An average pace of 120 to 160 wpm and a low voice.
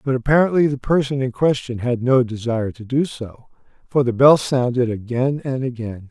No: average, 185 wpm; low, 125 Hz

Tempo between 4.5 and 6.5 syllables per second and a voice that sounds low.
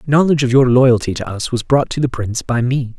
Yes: 6.0 syllables/s; low, 125 Hz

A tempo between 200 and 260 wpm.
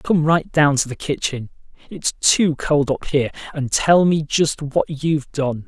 No: average, 170 wpm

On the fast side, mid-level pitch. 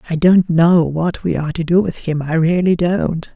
Yes: fast, 230 wpm; medium, 170 Hz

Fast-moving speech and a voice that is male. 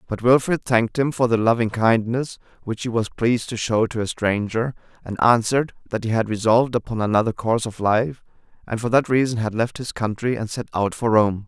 Yes: fast, 215 wpm; male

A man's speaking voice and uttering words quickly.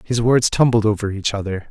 Yes: male; fast, 210 wpm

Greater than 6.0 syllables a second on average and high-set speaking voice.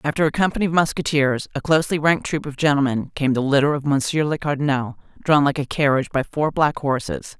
No: 6.2 syllables/s; medium, 145 Hz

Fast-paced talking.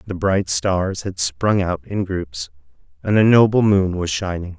No: average, 185 wpm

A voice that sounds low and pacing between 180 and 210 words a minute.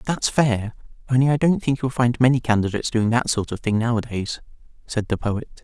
Yes: low, 120 Hz; average, 200 wpm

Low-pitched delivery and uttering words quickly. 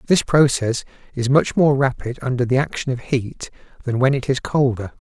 No: low, 130 Hz; average, 190 wpm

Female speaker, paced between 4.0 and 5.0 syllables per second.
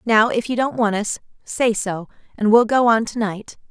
Yes: female; 4.8 syllables/s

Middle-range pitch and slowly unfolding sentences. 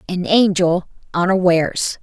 Yes: medium, 180 Hz; slow, 90 wpm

